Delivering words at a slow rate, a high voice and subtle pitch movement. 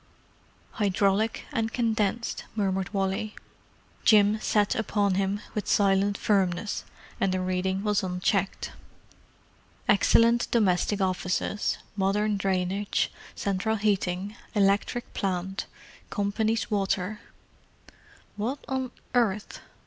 Yes: slow, 95 wpm; high, 200 Hz; narrow, 2.0 semitones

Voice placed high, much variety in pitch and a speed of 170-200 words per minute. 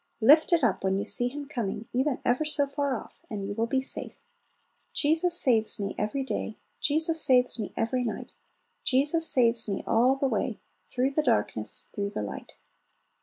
No: very high, 250 Hz; average, 4.5 semitones; average, 180 wpm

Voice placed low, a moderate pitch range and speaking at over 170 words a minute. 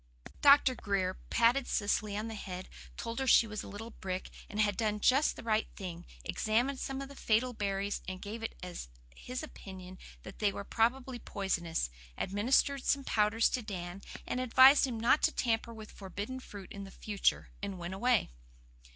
No: high, 215 Hz; average, 4.1 semitones; average, 180 wpm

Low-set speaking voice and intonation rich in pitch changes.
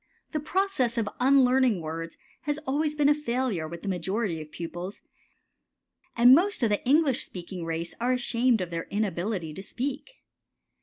No: high, 230 Hz; wide, 7.5 semitones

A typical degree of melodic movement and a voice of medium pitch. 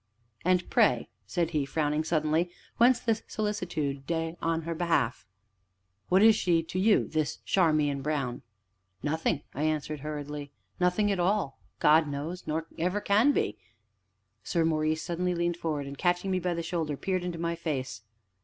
Yes: average, 3.1 semitones; medium, 165 Hz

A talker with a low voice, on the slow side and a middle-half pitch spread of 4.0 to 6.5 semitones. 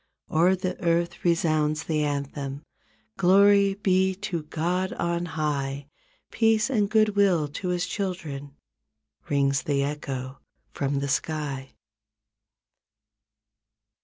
No: medium, 160 Hz; slow, 105 wpm; average, 4.8 semitones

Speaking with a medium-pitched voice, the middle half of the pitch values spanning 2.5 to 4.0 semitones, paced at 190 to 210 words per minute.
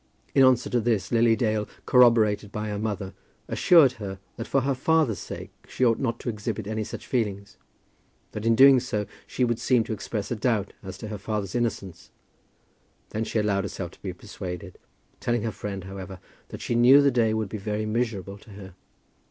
No: low, 110 Hz; average, 2.9 semitones; average, 195 wpm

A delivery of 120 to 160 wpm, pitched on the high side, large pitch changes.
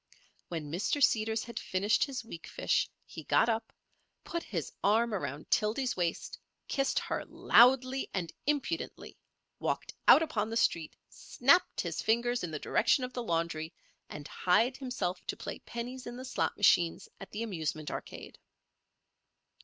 Yes: average, 150 wpm; high, 225 Hz; wide, 6.4 semitones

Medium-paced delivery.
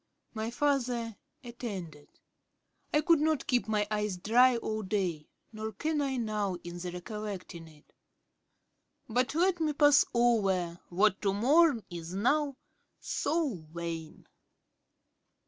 No: slow, 125 wpm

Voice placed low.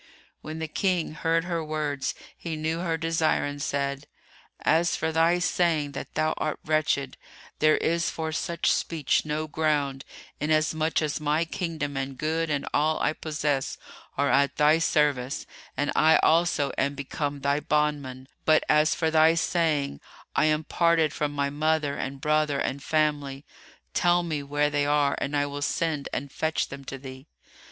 No: medium, 150 Hz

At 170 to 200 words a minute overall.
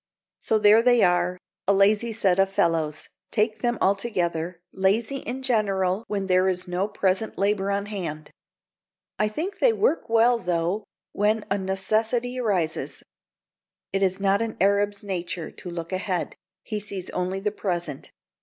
No: average, 155 wpm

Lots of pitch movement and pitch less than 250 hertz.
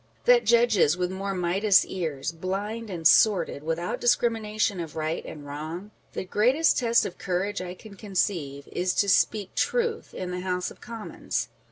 No: average, 3.9 semitones; high, 190 Hz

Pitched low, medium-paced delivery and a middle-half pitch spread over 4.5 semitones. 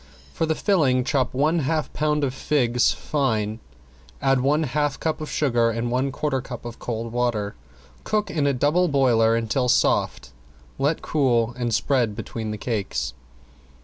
No: low, 130 Hz; average, 160 wpm; average, 4.1 semitones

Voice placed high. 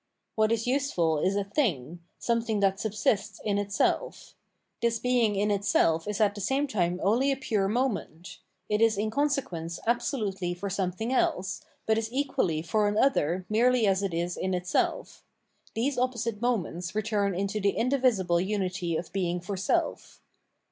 Yes: high, 205 Hz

